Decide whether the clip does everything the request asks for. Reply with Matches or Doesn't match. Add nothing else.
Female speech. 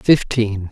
Doesn't match